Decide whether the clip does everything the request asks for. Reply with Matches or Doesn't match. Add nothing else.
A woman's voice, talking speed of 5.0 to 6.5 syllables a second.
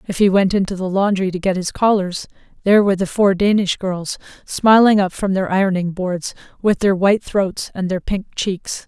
Matches